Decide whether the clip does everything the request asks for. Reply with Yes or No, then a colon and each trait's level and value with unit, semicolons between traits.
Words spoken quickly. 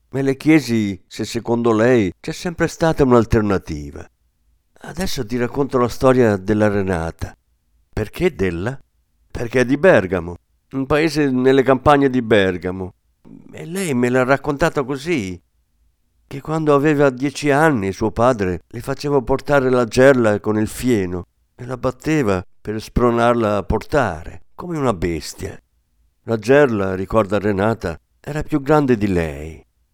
No: average, 140 wpm